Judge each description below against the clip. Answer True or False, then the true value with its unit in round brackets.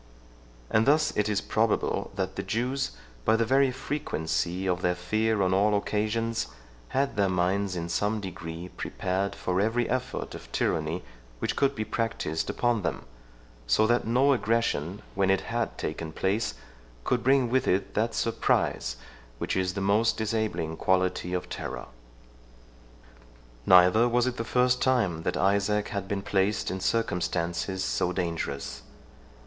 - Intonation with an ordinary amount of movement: True (4.2 semitones)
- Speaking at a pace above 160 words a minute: False (155 wpm)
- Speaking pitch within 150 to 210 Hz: False (100 Hz)